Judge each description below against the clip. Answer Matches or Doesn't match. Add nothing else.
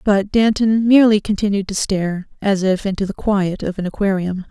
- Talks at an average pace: Matches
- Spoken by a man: Doesn't match